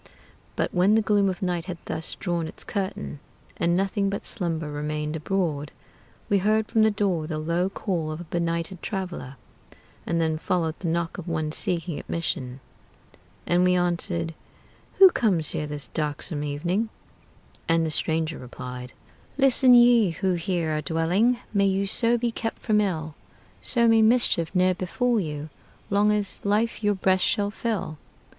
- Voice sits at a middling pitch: Yes, medium, 175 Hz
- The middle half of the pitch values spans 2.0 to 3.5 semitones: No, average, 4.3 semitones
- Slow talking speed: No, average, 165 wpm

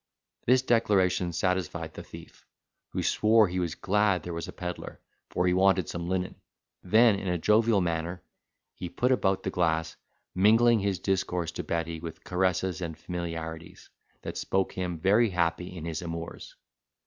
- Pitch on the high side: No, very low, 90 Hz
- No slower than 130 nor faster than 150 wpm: No, average, 160 wpm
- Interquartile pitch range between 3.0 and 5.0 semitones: No, narrow, 2.6 semitones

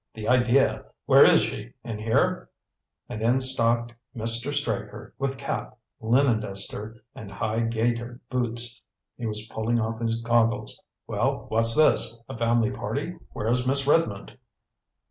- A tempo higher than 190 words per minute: No, average, 140 wpm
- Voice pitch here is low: Yes, low, 115 Hz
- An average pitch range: No, narrow, 2.1 semitones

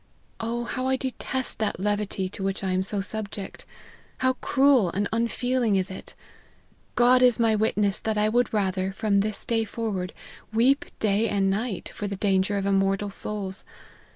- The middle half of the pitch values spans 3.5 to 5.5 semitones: No, average, 3.1 semitones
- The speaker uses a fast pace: No, average, 170 wpm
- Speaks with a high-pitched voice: Yes, high, 210 Hz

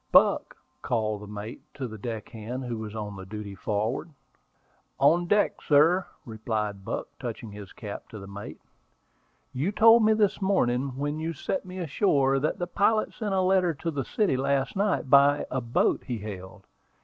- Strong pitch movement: Yes, wide, 8.4 semitones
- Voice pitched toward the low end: Yes, low, 130 Hz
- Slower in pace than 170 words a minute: No, average, 175 wpm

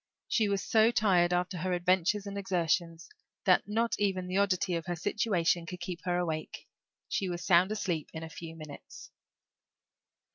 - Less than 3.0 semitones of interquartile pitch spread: Yes, narrow, 2.6 semitones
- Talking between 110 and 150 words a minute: No, average, 170 wpm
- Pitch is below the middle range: No, medium, 180 Hz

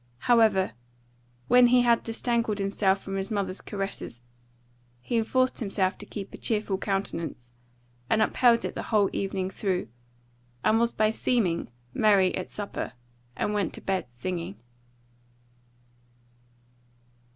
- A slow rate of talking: Yes, slow, 130 wpm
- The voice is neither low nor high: No, high, 200 Hz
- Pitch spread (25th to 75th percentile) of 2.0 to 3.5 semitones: Yes, average, 3.0 semitones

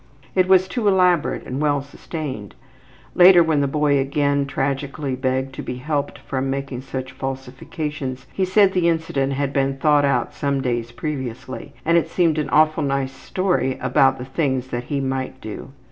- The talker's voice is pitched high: No, medium, 140 Hz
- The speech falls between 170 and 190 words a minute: Yes, average, 175 wpm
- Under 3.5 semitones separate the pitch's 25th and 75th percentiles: Yes, average, 2.9 semitones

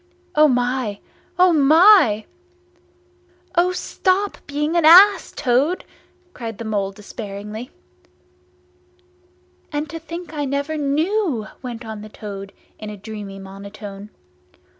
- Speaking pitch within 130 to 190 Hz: No, very high, 255 Hz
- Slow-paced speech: Yes, slow, 115 wpm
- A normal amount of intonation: No, wide, 7.6 semitones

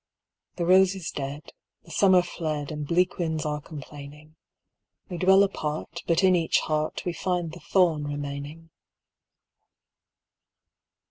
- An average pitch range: Yes, average, 3.2 semitones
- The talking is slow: Yes, slow, 130 wpm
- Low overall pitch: No, medium, 160 Hz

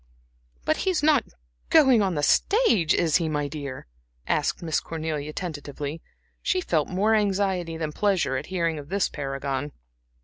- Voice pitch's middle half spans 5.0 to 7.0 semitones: Yes, average, 5.3 semitones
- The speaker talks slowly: No, average, 160 wpm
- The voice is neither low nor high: Yes, medium, 165 Hz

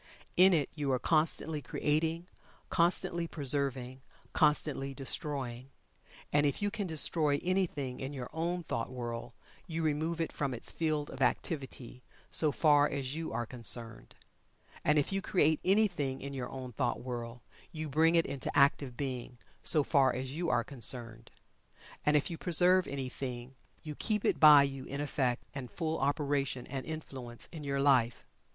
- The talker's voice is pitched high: No, medium, 140 Hz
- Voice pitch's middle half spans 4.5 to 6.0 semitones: No, average, 3.7 semitones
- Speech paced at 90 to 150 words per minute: No, average, 160 wpm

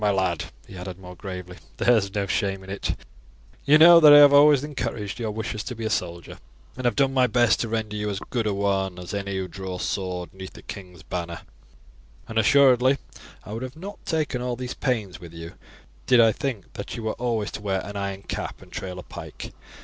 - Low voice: Yes, low, 105 Hz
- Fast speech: Yes, fast, 225 wpm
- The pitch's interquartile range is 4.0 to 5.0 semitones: Yes, average, 4.7 semitones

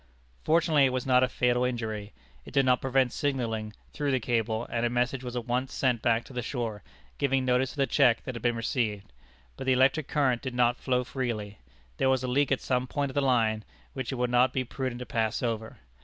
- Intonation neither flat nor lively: No, narrow, 2.0 semitones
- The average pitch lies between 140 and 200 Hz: No, low, 125 Hz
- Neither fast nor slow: No, fast, 230 wpm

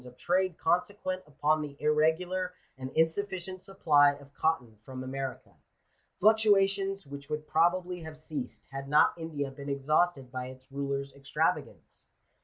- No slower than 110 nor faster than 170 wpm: Yes, average, 140 wpm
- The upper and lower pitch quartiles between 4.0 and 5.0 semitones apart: Yes, average, 4.7 semitones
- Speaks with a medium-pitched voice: Yes, medium, 155 Hz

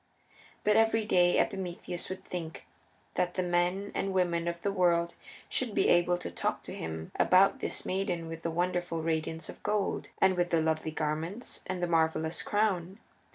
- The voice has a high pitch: No, medium, 175 Hz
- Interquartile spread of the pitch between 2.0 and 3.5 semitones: Yes, narrow, 2.4 semitones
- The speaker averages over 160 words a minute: Yes, average, 175 wpm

